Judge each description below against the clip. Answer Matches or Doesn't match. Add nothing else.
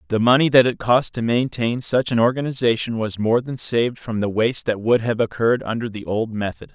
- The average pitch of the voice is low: Matches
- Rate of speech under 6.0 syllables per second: Matches